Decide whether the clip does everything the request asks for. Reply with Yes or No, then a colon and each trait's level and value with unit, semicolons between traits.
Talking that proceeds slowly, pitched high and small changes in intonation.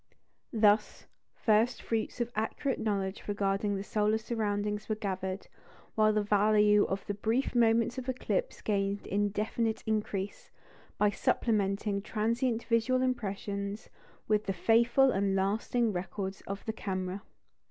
Yes: slow, 130 wpm; high, 210 Hz; narrow, 2.2 semitones